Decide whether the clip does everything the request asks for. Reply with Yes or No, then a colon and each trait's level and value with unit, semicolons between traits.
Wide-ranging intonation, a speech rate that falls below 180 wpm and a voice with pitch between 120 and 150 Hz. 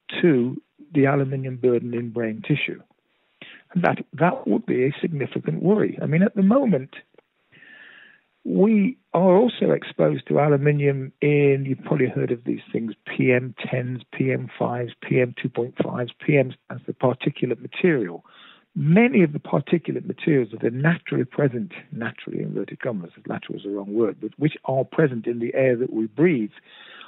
Yes: wide, 5.7 semitones; average, 150 wpm; medium, 140 Hz